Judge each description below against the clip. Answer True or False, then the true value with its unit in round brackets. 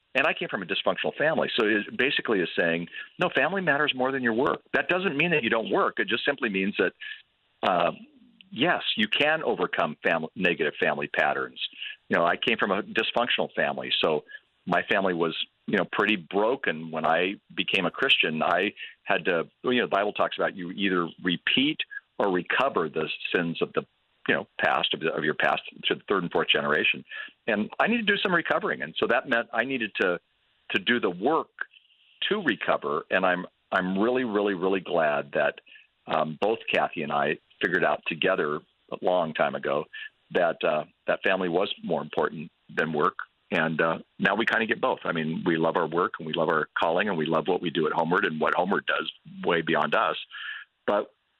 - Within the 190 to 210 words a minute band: True (205 wpm)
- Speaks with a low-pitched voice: False (195 Hz)